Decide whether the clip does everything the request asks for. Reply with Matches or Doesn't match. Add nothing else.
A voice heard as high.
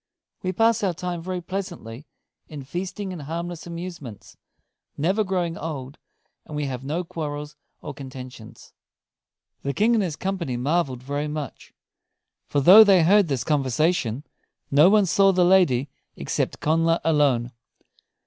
Doesn't match